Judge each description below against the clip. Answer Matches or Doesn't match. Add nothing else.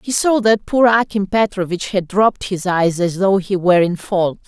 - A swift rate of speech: Matches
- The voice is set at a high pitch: Matches